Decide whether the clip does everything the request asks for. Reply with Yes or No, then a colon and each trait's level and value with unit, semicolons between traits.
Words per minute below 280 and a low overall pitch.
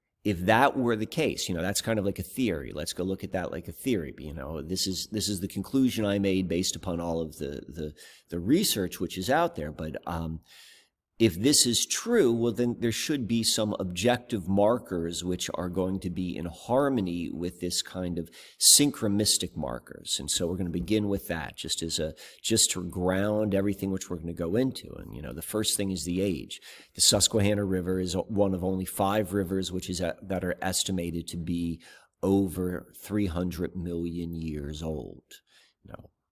Yes: fast, 205 wpm; very low, 95 Hz